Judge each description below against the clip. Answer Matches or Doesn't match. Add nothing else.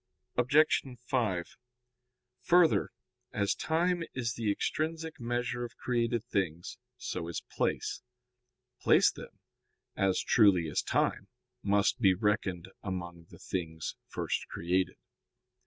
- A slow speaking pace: Matches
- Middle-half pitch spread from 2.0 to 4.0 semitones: Doesn't match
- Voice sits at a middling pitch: Doesn't match